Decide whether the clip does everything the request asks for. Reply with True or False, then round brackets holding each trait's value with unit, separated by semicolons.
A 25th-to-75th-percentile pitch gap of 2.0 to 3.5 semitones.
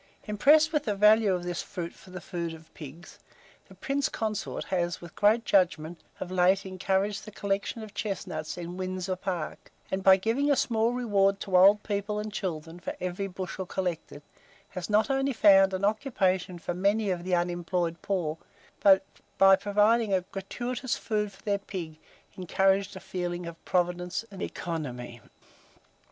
True (2.9 semitones)